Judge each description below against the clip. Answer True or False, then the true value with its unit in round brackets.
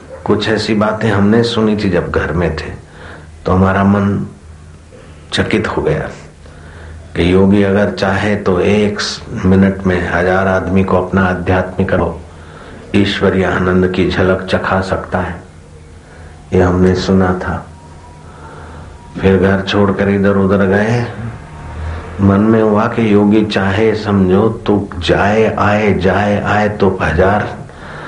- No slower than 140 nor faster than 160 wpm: False (130 wpm)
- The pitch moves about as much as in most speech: True (3.1 semitones)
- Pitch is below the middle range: True (95 Hz)